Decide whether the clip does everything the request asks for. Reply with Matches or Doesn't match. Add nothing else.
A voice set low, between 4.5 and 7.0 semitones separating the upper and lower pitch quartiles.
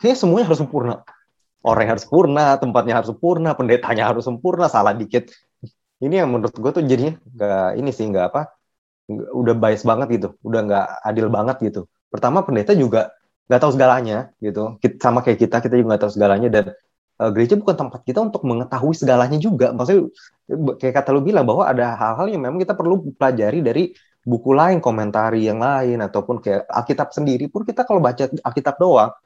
Matches